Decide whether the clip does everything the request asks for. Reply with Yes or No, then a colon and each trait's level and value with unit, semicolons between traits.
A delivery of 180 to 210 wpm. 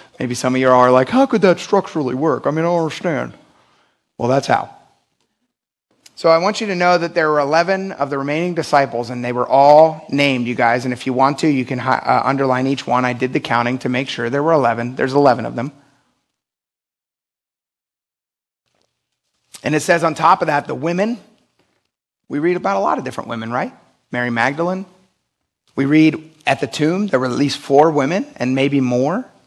Yes: fast, 205 wpm